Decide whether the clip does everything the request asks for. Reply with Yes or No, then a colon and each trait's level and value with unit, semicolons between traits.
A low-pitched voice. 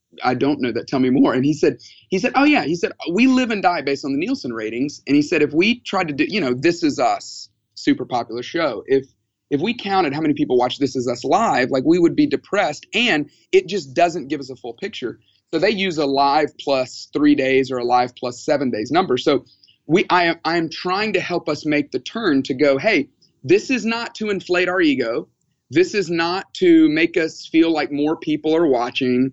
No: medium, 160 Hz